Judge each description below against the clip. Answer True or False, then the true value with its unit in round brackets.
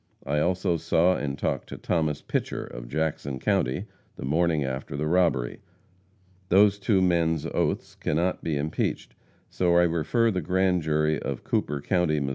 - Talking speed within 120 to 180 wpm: True (160 wpm)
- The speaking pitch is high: False (80 Hz)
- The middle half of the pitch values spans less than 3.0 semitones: False (3.7 semitones)